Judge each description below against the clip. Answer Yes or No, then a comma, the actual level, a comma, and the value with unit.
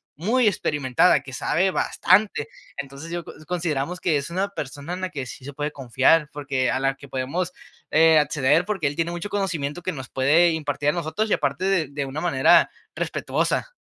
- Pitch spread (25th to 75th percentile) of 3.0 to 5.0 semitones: Yes, average, 4.2 semitones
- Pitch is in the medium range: Yes, medium, 155 Hz